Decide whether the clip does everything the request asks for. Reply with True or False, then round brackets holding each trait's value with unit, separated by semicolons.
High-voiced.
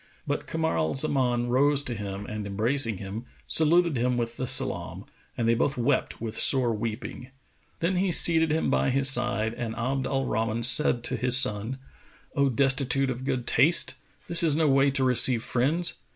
False (130 Hz)